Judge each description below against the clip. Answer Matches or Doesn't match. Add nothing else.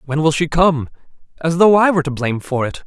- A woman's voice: Doesn't match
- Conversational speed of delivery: Doesn't match